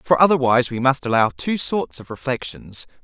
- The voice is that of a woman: No, male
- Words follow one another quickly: No, average, 180 wpm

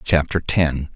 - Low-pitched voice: Yes, very low, 75 Hz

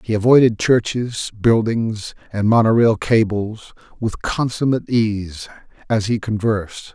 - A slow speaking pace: Yes, slow, 120 wpm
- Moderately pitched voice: No, low, 110 Hz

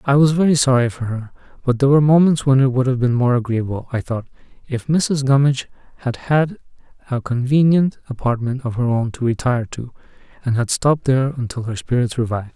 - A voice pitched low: Yes, low, 130 Hz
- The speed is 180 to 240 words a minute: Yes, average, 195 wpm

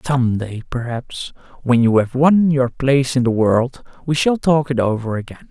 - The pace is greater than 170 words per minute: Yes, average, 195 wpm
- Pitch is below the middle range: Yes, low, 130 Hz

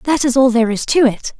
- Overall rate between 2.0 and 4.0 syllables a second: No, 6.4 syllables/s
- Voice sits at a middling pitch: No, very high, 250 Hz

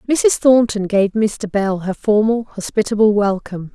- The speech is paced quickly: No, average, 145 wpm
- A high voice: Yes, high, 210 Hz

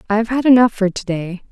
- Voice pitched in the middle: No, high, 215 Hz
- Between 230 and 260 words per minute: Yes, fast, 240 wpm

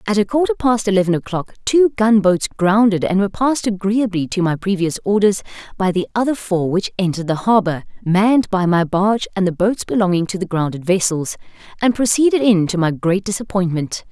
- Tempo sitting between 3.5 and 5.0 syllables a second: No, 5.6 syllables/s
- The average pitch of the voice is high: Yes, high, 195 Hz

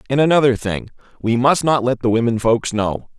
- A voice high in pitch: No, low, 120 Hz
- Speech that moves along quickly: No, average, 190 wpm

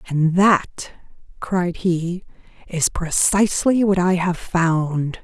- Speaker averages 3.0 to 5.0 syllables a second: Yes, 3.2 syllables/s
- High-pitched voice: No, medium, 180 Hz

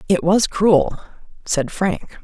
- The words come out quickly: No, slow, 135 wpm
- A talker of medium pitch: Yes, medium, 180 Hz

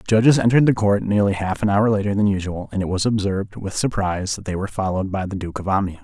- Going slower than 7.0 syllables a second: No, 7.1 syllables/s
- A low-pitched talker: Yes, low, 100 Hz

